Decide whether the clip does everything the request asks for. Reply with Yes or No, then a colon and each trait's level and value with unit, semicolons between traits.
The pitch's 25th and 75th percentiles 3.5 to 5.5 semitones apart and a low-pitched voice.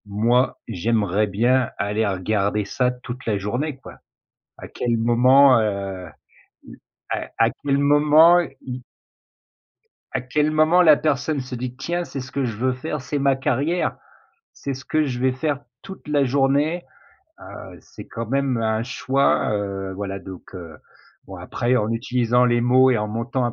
Yes: average, 4.2 semitones; low, 125 Hz